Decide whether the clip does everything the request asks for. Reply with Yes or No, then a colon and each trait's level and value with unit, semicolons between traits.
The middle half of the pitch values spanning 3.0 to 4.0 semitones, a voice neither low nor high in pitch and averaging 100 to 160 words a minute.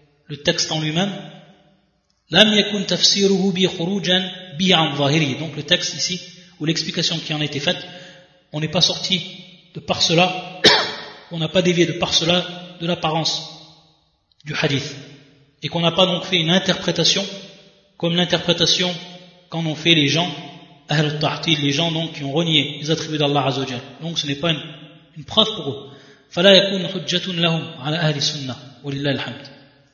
Yes: average, 3.3 semitones; medium, 165 Hz; average, 150 wpm